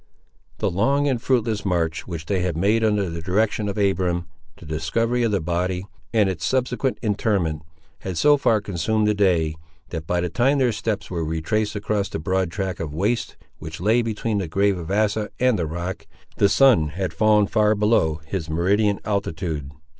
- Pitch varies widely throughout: No, average, 4.2 semitones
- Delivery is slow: No, average, 185 wpm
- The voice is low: Yes, low, 100 Hz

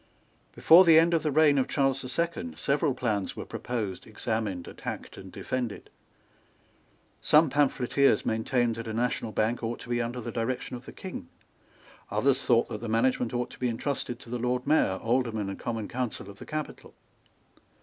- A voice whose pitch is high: No, low, 125 Hz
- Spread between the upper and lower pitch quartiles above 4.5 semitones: No, average, 3.2 semitones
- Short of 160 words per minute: No, average, 180 wpm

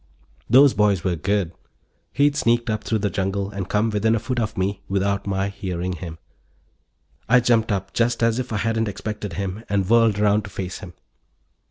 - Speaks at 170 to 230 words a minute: Yes, average, 190 wpm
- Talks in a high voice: No, low, 105 Hz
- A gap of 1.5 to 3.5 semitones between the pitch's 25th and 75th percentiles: Yes, average, 2.8 semitones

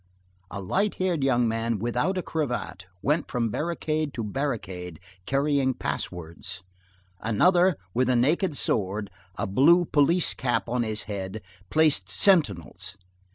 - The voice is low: Yes, low, 125 Hz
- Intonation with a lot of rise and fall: Yes, wide, 7.3 semitones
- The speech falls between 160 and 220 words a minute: No, slow, 135 wpm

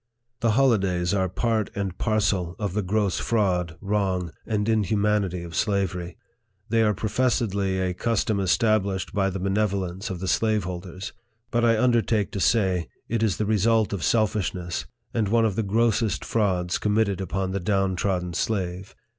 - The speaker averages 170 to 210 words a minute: No, average, 160 wpm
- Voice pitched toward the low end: Yes, low, 100 Hz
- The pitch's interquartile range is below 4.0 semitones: Yes, average, 2.8 semitones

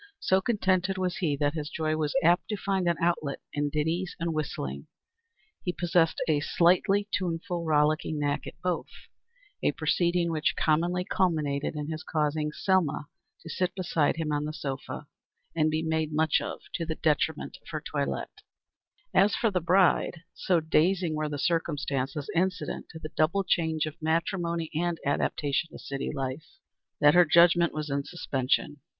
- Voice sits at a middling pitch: Yes, medium, 160 Hz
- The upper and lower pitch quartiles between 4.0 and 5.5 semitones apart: No, average, 2.7 semitones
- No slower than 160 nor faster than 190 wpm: Yes, average, 165 wpm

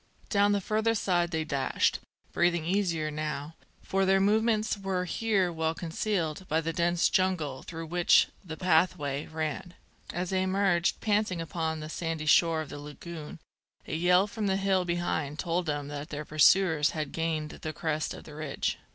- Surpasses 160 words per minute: Yes, average, 170 wpm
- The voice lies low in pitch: No, medium, 170 Hz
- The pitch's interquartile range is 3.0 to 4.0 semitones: Yes, average, 3.3 semitones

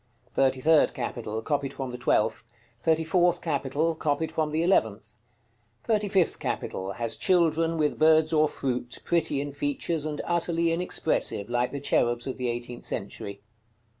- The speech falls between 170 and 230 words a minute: No, average, 155 wpm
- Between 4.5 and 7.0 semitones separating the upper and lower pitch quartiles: Yes, average, 4.9 semitones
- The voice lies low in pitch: No, medium, 145 Hz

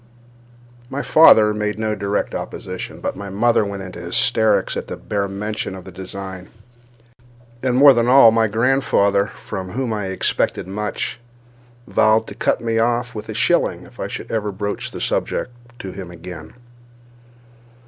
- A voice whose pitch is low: Yes, low, 105 Hz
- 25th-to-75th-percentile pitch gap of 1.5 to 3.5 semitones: Yes, average, 2.9 semitones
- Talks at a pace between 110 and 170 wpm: Yes, average, 160 wpm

